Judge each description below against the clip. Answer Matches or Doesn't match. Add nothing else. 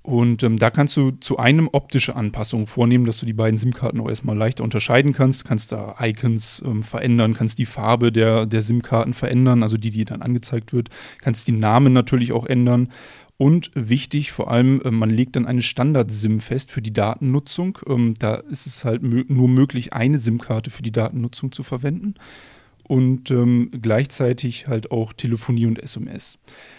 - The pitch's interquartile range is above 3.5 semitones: Doesn't match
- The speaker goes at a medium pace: Matches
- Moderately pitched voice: Doesn't match